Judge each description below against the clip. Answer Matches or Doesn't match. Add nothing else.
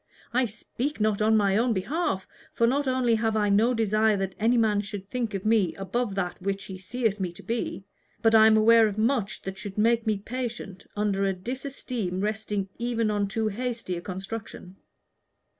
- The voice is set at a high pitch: Matches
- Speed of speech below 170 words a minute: Doesn't match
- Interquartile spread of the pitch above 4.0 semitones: Doesn't match